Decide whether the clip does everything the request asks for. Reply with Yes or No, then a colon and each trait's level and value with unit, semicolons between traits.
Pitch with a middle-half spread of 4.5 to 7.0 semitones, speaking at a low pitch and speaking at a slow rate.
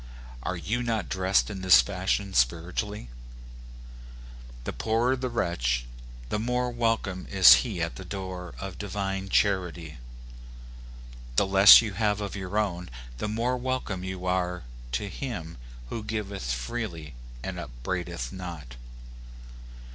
No: average, 3.5 semitones; very low, 95 Hz; slow, 130 wpm